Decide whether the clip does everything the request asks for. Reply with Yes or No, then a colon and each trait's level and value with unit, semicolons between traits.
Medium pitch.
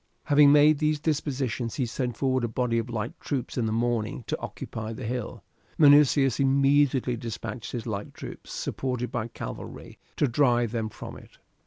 No: low, 125 Hz